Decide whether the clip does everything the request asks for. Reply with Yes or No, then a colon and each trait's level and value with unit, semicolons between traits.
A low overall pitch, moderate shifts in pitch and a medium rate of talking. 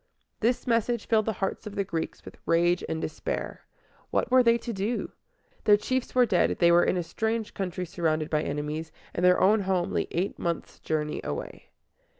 No: high, 190 Hz; average, 4.9 semitones; average, 190 wpm